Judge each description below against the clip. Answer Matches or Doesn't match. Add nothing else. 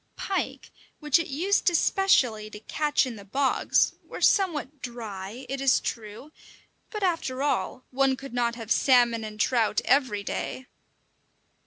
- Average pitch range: Matches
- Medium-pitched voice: Doesn't match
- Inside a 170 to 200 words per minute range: Doesn't match